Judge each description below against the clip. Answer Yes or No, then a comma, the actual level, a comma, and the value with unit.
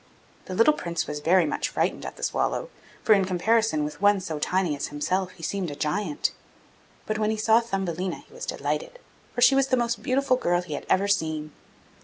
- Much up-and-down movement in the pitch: Yes, wide, 5.8 semitones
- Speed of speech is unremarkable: No, fast, 210 wpm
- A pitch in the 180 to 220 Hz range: Yes, high, 190 Hz